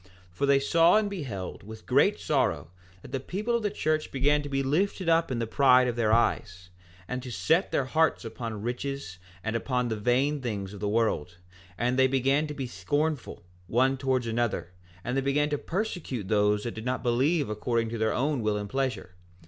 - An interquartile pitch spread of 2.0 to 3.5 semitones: No, average, 4.6 semitones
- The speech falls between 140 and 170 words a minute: No, fast, 205 wpm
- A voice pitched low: Yes, low, 125 Hz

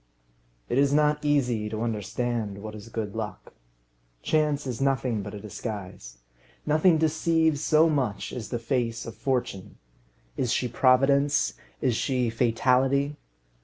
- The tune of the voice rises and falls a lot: No, average, 4.5 semitones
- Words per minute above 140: No, slow, 135 wpm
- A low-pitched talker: Yes, low, 125 Hz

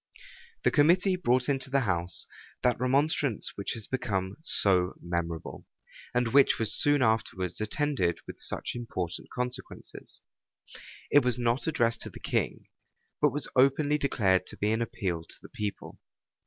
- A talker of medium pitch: No, low, 120 Hz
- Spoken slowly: No, average, 150 wpm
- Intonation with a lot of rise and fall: Yes, wide, 6.3 semitones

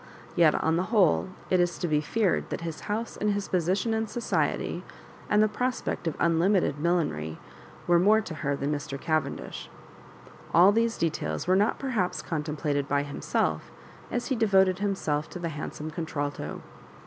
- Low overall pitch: No, medium, 175 Hz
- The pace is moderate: Yes, average, 165 wpm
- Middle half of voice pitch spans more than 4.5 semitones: Yes, average, 5.1 semitones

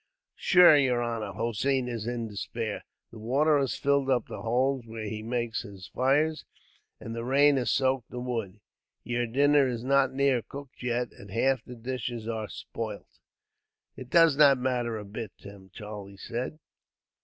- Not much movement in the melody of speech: No, average, 3.2 semitones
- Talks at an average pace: Yes, average, 165 wpm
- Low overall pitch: Yes, low, 120 Hz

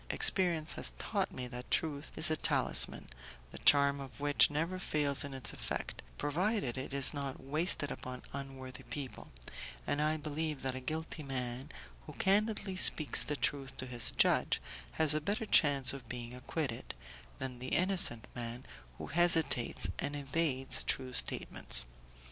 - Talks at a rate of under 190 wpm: Yes, average, 155 wpm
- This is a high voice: No, medium, 140 Hz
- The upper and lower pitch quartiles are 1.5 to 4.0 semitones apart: Yes, average, 3.5 semitones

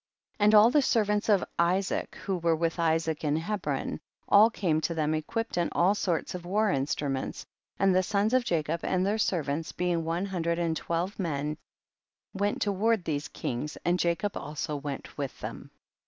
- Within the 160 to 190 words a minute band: Yes, average, 185 wpm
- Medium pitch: Yes, medium, 175 Hz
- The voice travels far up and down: No, average, 4.3 semitones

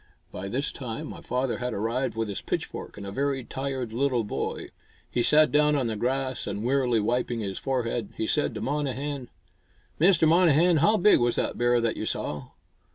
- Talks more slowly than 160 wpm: No, average, 190 wpm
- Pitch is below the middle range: Yes, low, 125 Hz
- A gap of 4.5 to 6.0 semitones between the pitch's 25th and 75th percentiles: No, average, 3.8 semitones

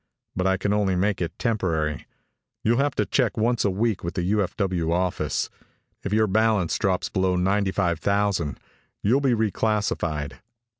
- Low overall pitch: Yes, low, 100 Hz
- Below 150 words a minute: No, average, 160 wpm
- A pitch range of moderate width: Yes, average, 3.1 semitones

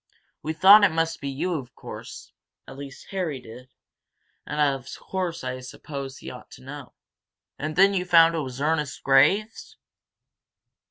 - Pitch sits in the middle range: Yes, medium, 150 Hz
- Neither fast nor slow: Yes, average, 160 wpm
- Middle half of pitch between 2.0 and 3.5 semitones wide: No, average, 4.6 semitones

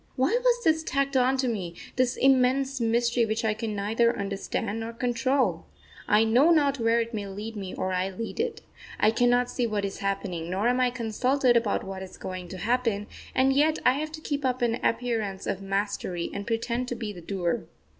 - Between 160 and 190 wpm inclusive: No, fast, 205 wpm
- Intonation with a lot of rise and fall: No, average, 4.1 semitones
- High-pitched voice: Yes, high, 230 Hz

